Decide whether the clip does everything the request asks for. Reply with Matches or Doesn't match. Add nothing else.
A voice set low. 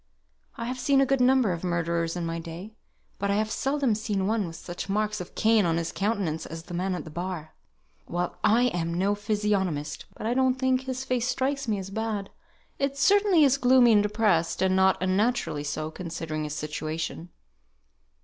Doesn't match